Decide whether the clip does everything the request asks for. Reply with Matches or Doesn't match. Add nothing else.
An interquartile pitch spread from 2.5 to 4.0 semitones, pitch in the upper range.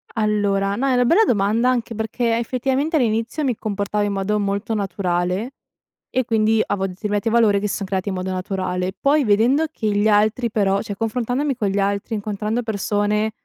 Matches